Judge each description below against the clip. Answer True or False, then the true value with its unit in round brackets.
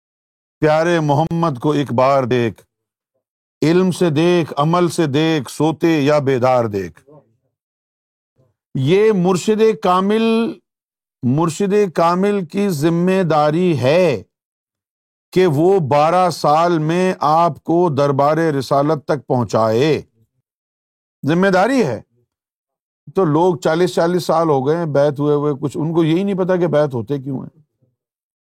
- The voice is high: False (155 Hz)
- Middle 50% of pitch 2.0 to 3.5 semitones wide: False (4.6 semitones)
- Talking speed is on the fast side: False (130 wpm)